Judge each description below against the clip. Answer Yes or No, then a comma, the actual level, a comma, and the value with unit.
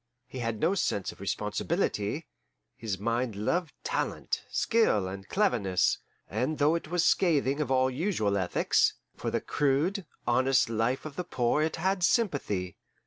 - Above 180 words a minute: No, average, 150 wpm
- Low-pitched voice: Yes, low, 130 Hz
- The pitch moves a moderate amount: No, wide, 7.3 semitones